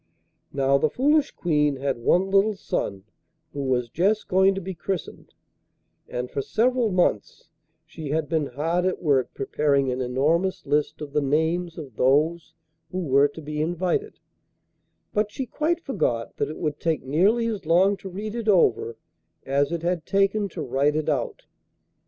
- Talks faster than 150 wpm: Yes, average, 170 wpm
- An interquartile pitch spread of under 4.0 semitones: No, wide, 5.5 semitones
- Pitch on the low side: No, medium, 160 Hz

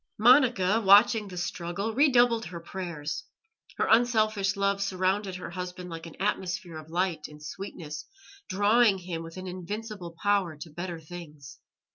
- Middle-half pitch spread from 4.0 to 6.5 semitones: No, average, 3.5 semitones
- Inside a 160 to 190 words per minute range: No, average, 145 wpm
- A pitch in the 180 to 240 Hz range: Yes, medium, 185 Hz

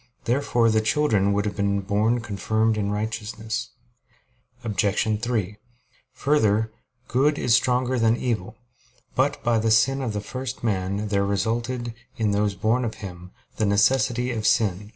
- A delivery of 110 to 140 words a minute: No, average, 150 wpm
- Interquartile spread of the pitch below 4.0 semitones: Yes, average, 2.7 semitones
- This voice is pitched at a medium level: No, low, 110 Hz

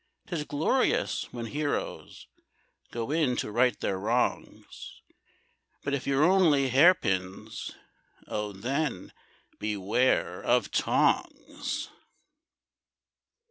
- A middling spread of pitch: No, wide, 5.9 semitones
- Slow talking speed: Yes, slow, 95 wpm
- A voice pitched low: Yes, low, 130 Hz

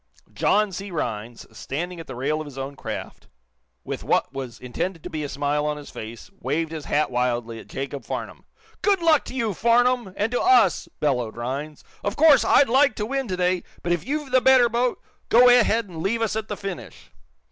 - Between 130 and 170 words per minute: No, average, 200 wpm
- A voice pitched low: No, medium, 180 Hz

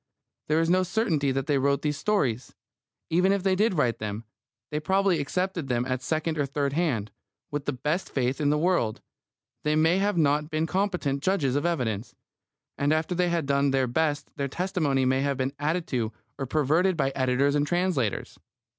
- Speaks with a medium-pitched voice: Yes, medium, 150 Hz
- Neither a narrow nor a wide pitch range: Yes, average, 4.4 semitones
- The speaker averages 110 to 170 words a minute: No, average, 190 wpm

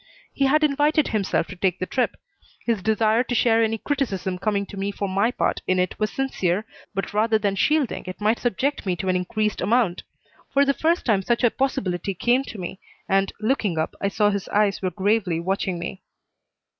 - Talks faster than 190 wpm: Yes, fast, 205 wpm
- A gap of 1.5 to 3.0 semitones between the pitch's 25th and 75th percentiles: No, average, 4.1 semitones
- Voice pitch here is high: Yes, high, 210 Hz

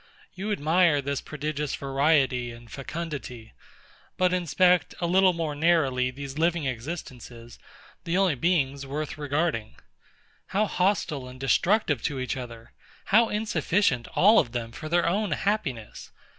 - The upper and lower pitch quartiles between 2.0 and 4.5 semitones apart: No, wide, 5.5 semitones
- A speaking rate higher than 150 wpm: No, slow, 135 wpm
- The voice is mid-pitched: Yes, medium, 150 Hz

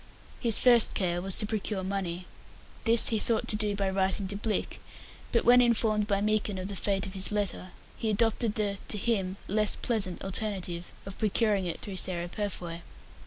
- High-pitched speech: Yes, high, 200 Hz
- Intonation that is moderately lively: No, narrow, 2.3 semitones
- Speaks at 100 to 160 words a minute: No, average, 185 wpm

